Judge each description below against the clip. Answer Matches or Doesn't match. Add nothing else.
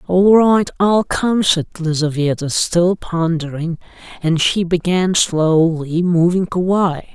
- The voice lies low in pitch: Doesn't match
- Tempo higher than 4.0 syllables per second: Doesn't match